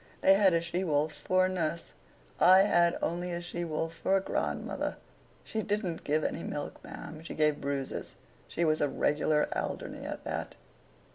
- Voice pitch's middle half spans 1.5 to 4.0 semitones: Yes, average, 3.2 semitones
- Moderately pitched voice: Yes, medium, 170 Hz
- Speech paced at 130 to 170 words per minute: No, average, 180 wpm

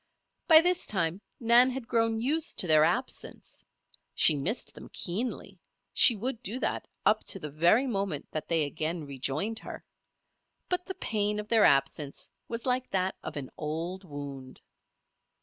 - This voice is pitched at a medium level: No, high, 195 Hz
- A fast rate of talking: No, average, 160 wpm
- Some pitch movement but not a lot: No, wide, 7.5 semitones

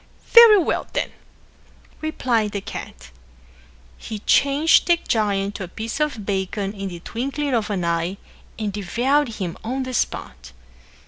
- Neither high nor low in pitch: No, high, 215 Hz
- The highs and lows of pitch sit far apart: Yes, wide, 5.9 semitones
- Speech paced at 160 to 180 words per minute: No, average, 145 wpm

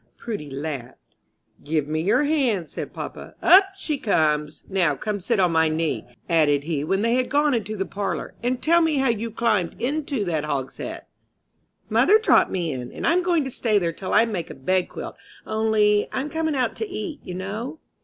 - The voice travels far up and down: Yes, wide, 8.5 semitones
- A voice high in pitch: Yes, high, 210 Hz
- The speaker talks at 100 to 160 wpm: No, average, 195 wpm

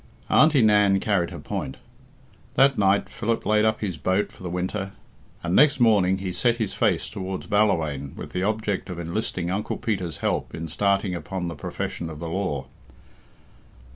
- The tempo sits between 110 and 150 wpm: No, average, 170 wpm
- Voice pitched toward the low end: Yes, very low, 95 Hz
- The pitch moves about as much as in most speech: Yes, average, 3.6 semitones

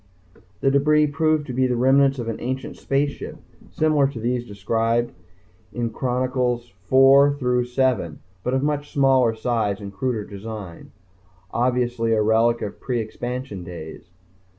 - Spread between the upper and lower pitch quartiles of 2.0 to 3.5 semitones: Yes, average, 3.1 semitones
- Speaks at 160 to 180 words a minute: No, average, 150 wpm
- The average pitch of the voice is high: No, low, 125 Hz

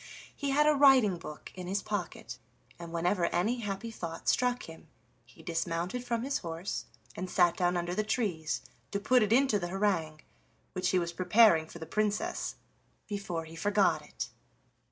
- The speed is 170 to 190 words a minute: Yes, average, 175 wpm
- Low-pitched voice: No, high, 190 Hz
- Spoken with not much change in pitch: No, average, 4.4 semitones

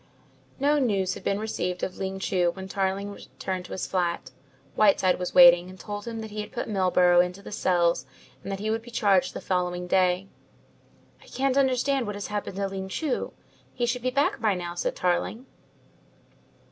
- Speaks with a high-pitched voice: Yes, high, 195 Hz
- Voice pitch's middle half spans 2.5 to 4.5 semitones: Yes, average, 3.3 semitones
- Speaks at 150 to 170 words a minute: No, average, 195 wpm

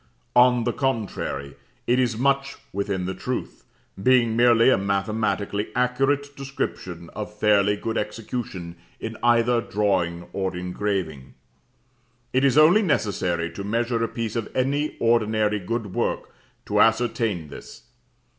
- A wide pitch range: No, average, 4.0 semitones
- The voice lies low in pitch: Yes, low, 110 Hz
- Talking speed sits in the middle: No, slow, 130 wpm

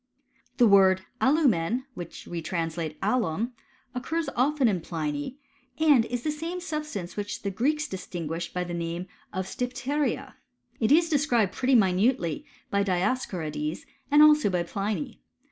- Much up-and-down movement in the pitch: Yes, wide, 7.7 semitones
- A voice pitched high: Yes, high, 210 Hz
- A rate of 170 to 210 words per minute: No, slow, 135 wpm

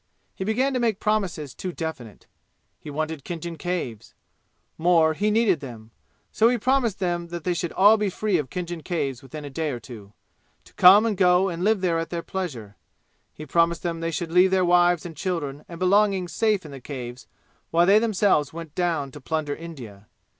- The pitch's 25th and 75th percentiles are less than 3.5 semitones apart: No, average, 4.0 semitones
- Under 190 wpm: No, average, 195 wpm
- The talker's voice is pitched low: No, medium, 170 Hz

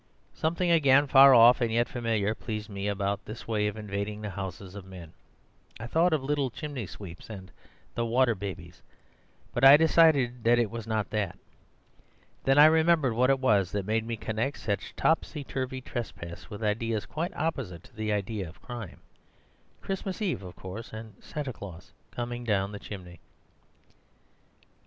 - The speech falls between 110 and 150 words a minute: No, average, 170 wpm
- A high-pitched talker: No, low, 115 Hz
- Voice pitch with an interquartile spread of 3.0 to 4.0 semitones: No, average, 4.8 semitones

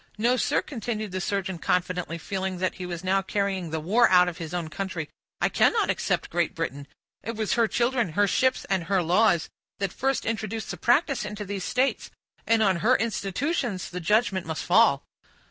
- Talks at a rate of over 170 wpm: Yes, average, 190 wpm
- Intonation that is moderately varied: Yes, average, 4.0 semitones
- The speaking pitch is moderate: No, high, 195 Hz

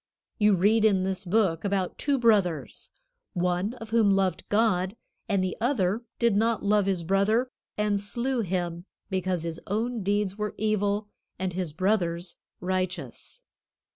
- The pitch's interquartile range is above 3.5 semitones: No, average, 2.9 semitones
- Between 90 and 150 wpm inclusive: Yes, average, 145 wpm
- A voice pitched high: Yes, high, 200 Hz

